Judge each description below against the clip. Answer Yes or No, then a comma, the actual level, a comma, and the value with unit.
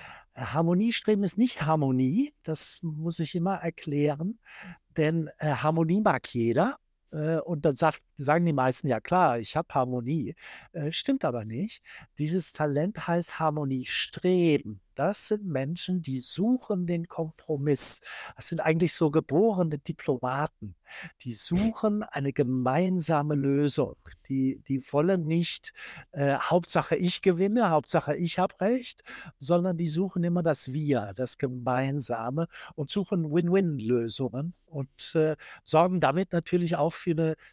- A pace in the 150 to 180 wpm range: No, average, 135 wpm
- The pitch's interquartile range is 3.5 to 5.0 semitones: Yes, average, 4.1 semitones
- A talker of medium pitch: Yes, medium, 160 Hz